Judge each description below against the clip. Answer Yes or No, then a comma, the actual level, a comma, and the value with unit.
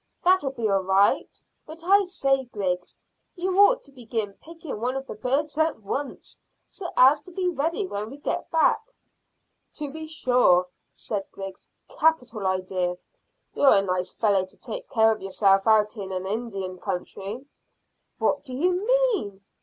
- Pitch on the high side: Yes, high, 245 Hz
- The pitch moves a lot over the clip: Yes, wide, 8.4 semitones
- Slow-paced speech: No, average, 160 wpm